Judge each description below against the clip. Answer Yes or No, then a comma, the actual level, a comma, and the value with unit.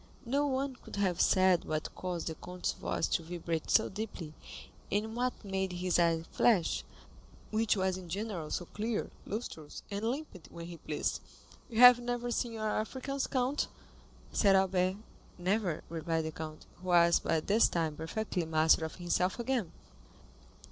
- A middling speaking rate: Yes, average, 160 wpm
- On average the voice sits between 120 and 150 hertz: No, medium, 185 Hz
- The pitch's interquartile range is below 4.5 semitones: No, average, 5.0 semitones